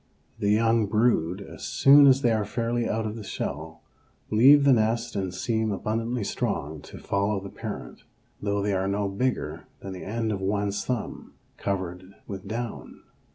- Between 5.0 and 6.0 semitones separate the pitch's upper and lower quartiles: No, average, 3.0 semitones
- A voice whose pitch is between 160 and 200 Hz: No, low, 105 Hz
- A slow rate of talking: No, average, 170 wpm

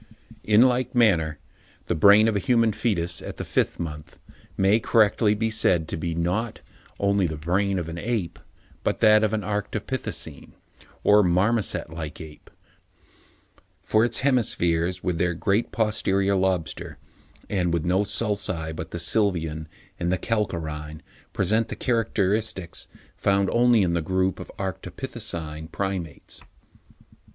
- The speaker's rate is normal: Yes, average, 145 wpm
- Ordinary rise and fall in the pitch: Yes, average, 4.2 semitones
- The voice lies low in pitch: Yes, very low, 95 Hz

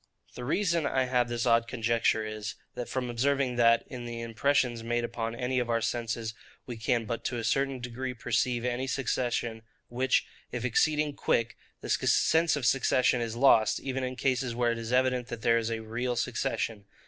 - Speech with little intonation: Yes, narrow, 1.9 semitones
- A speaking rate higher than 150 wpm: Yes, average, 190 wpm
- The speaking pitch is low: Yes, low, 120 Hz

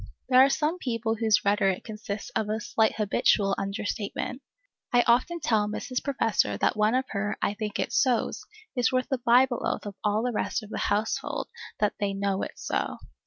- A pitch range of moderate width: Yes, average, 3.2 semitones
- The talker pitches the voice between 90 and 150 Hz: No, high, 220 Hz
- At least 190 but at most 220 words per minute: Yes, average, 195 wpm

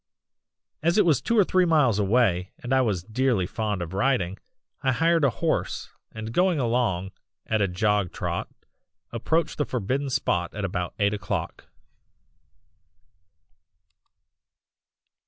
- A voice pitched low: Yes, low, 115 Hz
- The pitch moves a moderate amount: No, wide, 5.9 semitones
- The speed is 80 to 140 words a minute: Yes, slow, 135 wpm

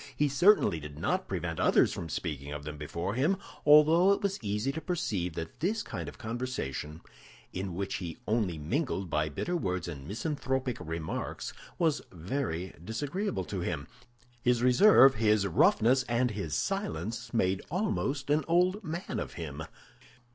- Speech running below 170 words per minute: Yes, average, 155 wpm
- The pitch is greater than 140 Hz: No, low, 115 Hz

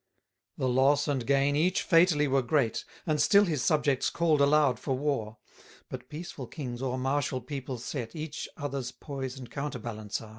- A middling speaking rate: Yes, average, 175 wpm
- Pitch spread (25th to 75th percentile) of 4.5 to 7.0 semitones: No, average, 2.7 semitones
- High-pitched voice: No, medium, 140 Hz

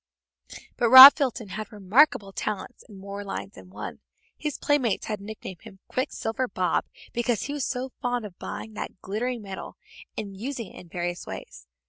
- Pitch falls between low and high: No, high, 215 Hz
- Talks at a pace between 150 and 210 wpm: Yes, average, 170 wpm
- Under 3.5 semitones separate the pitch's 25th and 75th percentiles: No, average, 4.6 semitones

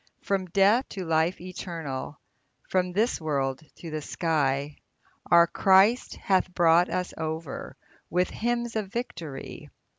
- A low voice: No, medium, 175 Hz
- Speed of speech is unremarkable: No, slow, 125 wpm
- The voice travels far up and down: No, average, 3.5 semitones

